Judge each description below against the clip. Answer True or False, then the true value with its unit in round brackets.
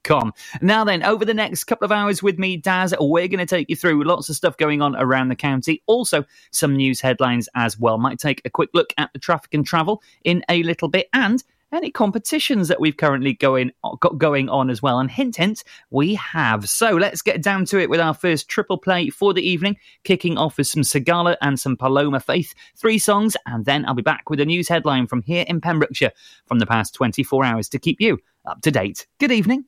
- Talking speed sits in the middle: False (230 wpm)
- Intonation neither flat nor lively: False (6.1 semitones)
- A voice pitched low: False (165 Hz)